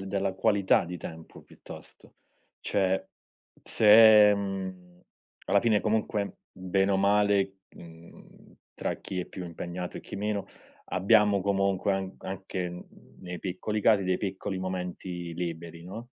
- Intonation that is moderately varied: No, narrow, 2.1 semitones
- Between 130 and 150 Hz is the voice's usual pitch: No, very low, 95 Hz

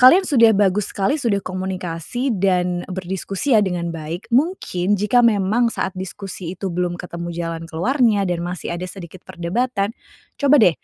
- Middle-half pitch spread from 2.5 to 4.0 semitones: No, average, 4.4 semitones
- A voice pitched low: No, high, 190 Hz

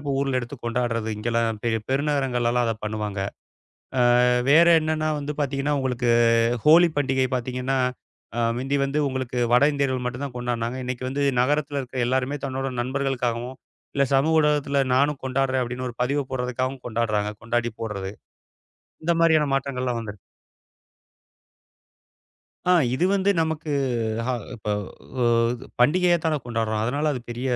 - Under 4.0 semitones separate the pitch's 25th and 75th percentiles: Yes, average, 3.0 semitones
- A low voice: Yes, low, 130 Hz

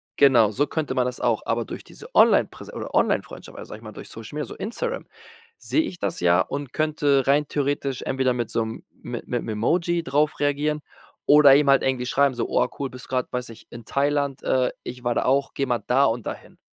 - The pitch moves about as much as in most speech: Yes, average, 3.0 semitones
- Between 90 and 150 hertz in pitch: Yes, low, 135 Hz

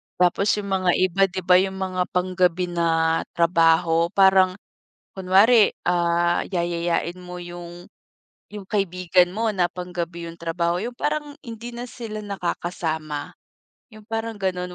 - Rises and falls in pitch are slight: Yes, narrow, 2.2 semitones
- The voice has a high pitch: No, medium, 180 Hz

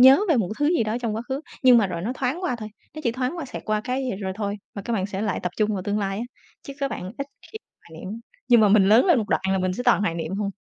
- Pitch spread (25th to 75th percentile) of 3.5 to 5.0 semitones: Yes, average, 4.5 semitones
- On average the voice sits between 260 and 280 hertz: No, high, 215 Hz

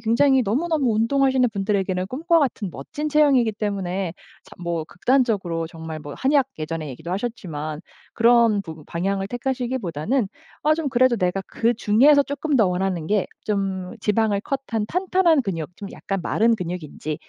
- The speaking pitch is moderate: No, high, 210 Hz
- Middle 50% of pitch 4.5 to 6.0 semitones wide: No, wide, 6.4 semitones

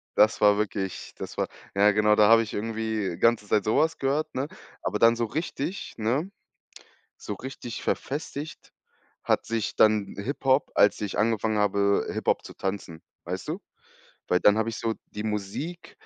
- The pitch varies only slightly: No, average, 3.4 semitones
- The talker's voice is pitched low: Yes, low, 110 Hz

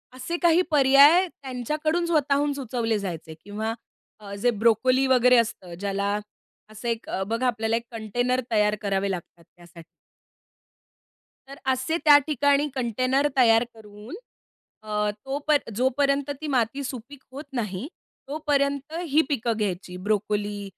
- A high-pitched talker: Yes, high, 245 Hz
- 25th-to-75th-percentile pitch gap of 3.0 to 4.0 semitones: No, average, 5.0 semitones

